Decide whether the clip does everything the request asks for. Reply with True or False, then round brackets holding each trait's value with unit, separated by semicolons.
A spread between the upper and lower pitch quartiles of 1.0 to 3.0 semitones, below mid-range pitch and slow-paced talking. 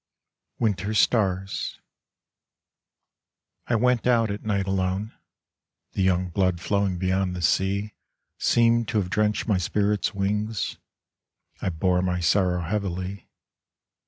True (2.5 semitones; 100 Hz; 115 wpm)